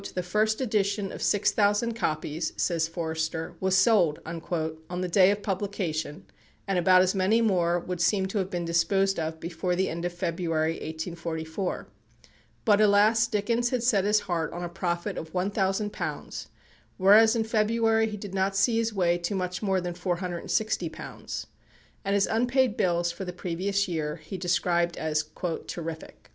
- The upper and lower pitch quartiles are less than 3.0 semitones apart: No, average, 3.4 semitones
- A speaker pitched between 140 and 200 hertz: Yes, medium, 185 Hz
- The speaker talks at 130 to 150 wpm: No, average, 165 wpm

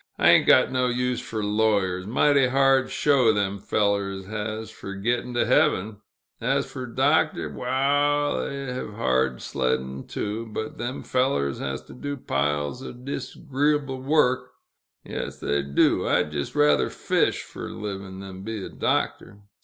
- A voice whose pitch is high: No, low, 110 Hz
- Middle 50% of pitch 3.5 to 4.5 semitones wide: No, average, 5.2 semitones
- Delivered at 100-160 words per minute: Yes, average, 150 wpm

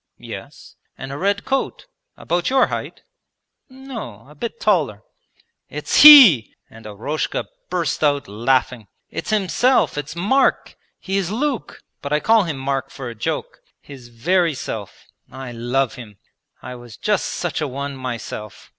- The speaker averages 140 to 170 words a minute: Yes, average, 150 wpm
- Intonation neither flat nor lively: No, wide, 8.4 semitones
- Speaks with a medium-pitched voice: Yes, medium, 145 Hz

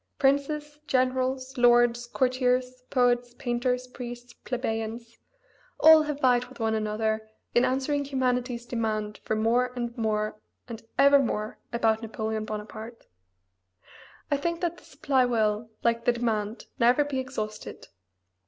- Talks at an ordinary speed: No, slow, 130 wpm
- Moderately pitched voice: No, high, 245 Hz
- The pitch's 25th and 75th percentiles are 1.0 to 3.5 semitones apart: Yes, average, 2.7 semitones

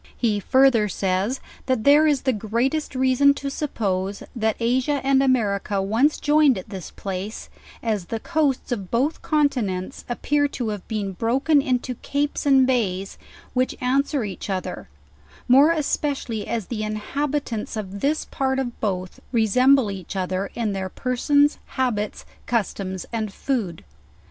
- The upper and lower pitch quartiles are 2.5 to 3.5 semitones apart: No, average, 5.2 semitones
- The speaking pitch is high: Yes, high, 240 Hz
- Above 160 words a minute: No, average, 145 wpm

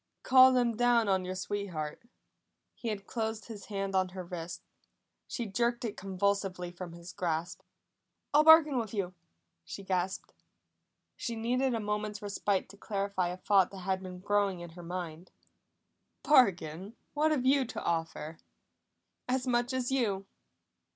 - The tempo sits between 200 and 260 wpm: No, average, 150 wpm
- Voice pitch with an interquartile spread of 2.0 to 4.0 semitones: No, average, 4.5 semitones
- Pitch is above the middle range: Yes, high, 200 Hz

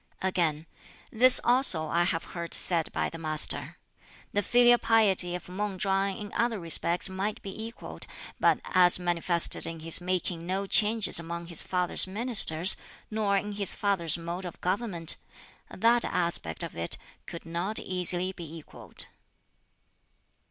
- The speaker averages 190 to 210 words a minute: No, average, 150 wpm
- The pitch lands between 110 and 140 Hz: No, medium, 185 Hz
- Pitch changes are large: No, average, 3.2 semitones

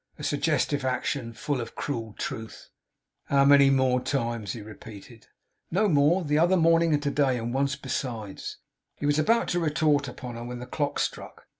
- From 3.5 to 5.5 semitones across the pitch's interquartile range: Yes, average, 3.8 semitones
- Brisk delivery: No, average, 185 wpm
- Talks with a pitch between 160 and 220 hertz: No, medium, 140 Hz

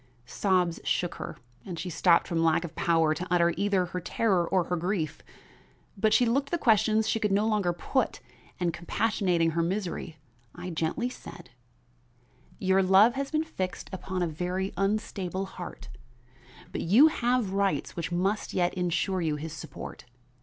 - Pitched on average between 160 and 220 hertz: Yes, medium, 185 Hz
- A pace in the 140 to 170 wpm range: Yes, average, 165 wpm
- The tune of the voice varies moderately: Yes, average, 3.5 semitones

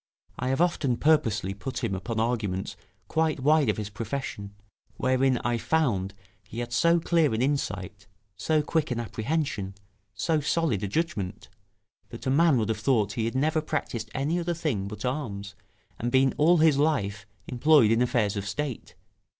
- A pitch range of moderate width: No, wide, 6.3 semitones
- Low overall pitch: Yes, low, 125 Hz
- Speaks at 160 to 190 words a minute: Yes, average, 170 wpm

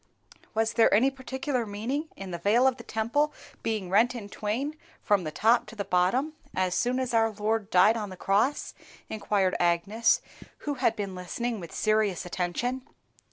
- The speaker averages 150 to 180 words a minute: Yes, average, 175 wpm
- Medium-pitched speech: No, high, 220 Hz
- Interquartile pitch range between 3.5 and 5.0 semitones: Yes, average, 4.0 semitones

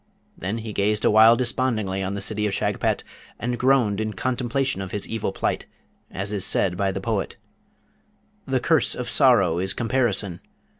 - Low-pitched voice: Yes, low, 105 Hz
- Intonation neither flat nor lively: Yes, average, 3.3 semitones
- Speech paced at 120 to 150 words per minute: No, average, 165 wpm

